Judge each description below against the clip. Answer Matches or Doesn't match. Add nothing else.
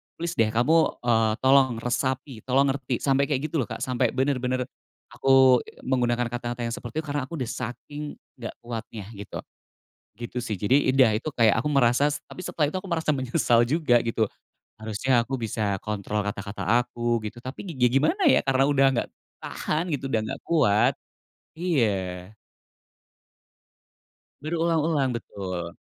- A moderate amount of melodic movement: Matches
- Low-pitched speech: Matches